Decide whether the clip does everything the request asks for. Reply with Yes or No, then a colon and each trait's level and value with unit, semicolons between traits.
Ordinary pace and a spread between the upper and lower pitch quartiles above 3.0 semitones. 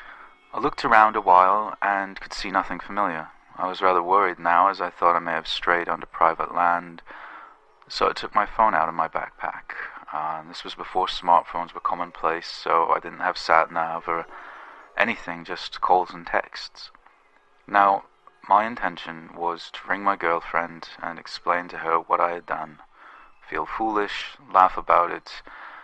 No: average, 170 wpm; average, 2.7 semitones